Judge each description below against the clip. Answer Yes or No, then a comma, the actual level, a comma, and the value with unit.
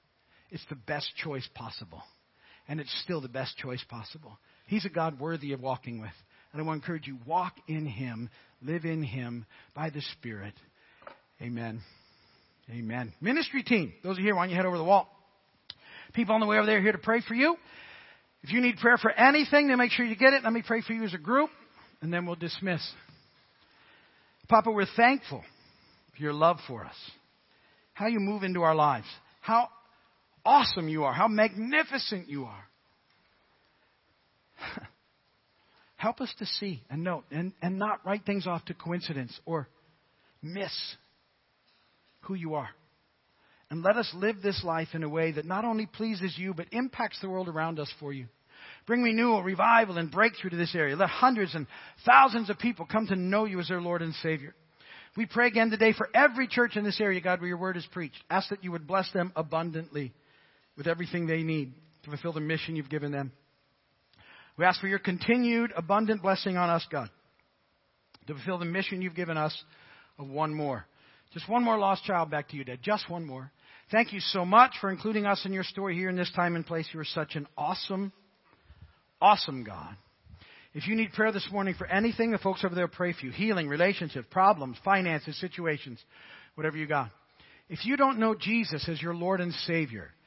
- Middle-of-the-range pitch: Yes, medium, 175 Hz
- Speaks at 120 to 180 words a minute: No, average, 195 wpm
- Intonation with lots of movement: Yes, wide, 5.7 semitones